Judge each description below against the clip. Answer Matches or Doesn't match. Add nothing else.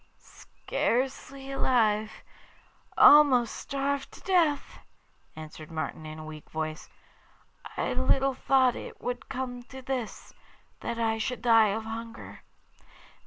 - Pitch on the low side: Doesn't match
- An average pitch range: Matches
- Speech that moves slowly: Matches